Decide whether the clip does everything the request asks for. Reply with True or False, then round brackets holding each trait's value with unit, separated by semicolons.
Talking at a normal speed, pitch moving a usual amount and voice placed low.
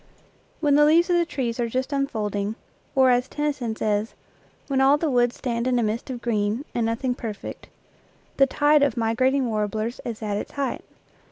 False (190 wpm; 3.7 semitones; 245 Hz)